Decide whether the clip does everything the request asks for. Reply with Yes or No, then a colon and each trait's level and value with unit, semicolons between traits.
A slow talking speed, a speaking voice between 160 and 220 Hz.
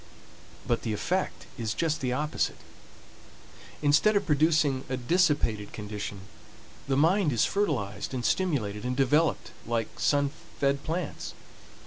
No: slow, 125 wpm; medium, 140 Hz